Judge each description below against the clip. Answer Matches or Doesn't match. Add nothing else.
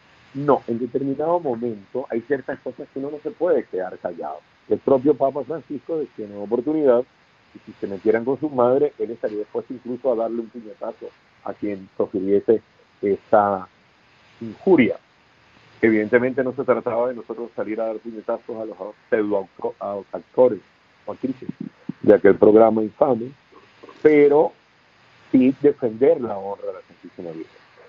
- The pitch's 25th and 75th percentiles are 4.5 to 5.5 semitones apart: Matches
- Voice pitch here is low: Matches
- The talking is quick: Doesn't match